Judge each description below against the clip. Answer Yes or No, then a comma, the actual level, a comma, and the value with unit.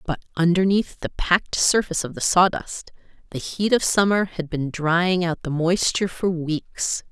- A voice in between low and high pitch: Yes, medium, 175 Hz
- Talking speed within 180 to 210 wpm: No, average, 170 wpm